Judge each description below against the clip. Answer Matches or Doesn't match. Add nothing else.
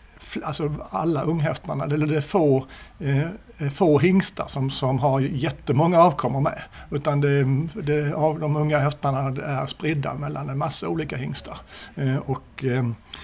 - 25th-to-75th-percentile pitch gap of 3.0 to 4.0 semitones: Doesn't match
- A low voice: Doesn't match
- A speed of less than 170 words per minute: Matches